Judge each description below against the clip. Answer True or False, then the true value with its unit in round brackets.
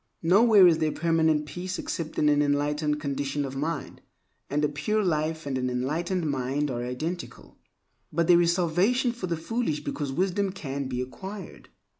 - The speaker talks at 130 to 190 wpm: True (170 wpm)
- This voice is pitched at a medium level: True (155 Hz)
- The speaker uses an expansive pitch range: False (3.8 semitones)